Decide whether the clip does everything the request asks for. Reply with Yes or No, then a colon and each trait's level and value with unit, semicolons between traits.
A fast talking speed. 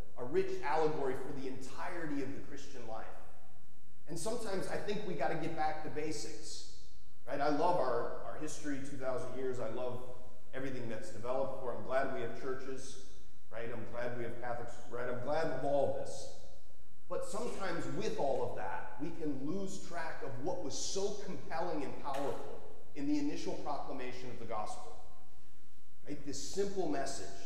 No: average, 175 wpm